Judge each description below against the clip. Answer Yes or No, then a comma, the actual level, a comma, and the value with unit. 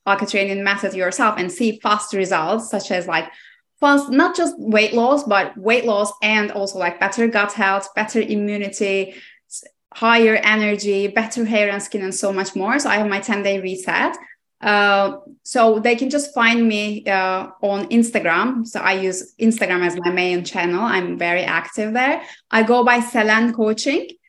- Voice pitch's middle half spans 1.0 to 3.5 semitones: Yes, average, 2.9 semitones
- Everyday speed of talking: Yes, average, 175 wpm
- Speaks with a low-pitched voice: No, high, 210 Hz